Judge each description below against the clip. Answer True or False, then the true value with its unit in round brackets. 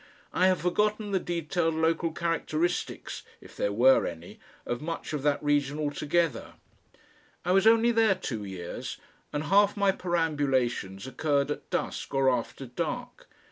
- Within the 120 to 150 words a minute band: True (145 wpm)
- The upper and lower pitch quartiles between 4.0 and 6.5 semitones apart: True (5.0 semitones)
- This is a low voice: False (155 Hz)